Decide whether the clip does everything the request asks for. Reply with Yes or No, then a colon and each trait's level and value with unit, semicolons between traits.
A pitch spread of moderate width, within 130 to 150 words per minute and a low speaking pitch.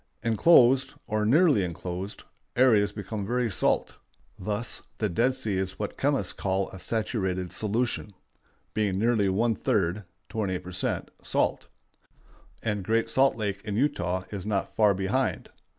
Yes: average, 3.5 semitones; average, 140 wpm; low, 105 Hz